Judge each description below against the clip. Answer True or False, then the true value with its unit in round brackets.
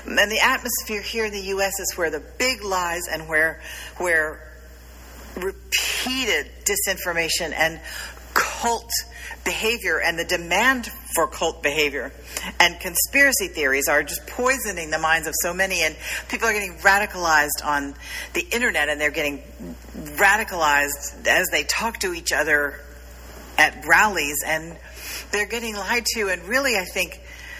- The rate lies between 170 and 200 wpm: False (145 wpm)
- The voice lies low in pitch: False (180 Hz)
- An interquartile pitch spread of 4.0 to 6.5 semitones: True (5.4 semitones)